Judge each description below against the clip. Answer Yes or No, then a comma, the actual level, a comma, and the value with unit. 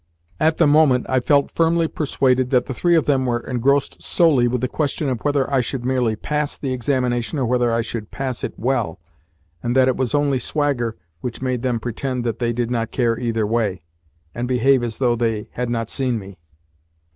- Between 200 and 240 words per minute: Yes, fast, 205 wpm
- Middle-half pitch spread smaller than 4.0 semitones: Yes, average, 2.7 semitones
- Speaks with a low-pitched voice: Yes, low, 125 Hz